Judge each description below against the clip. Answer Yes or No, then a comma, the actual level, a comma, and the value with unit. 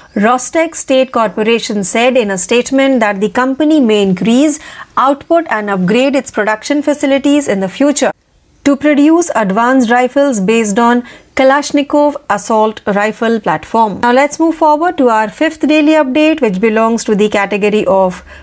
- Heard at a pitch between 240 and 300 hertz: Yes, high, 245 Hz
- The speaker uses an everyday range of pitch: Yes, average, 5.0 semitones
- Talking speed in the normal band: No, fast, 150 wpm